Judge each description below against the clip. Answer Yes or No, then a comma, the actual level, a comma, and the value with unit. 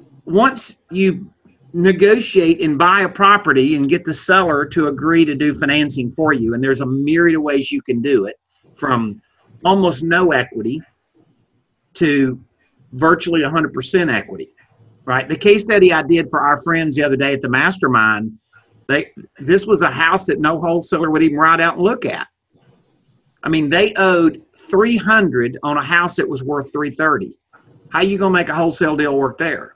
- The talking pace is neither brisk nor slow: Yes, average, 180 wpm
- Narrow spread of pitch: No, average, 4.8 semitones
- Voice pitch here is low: No, medium, 160 Hz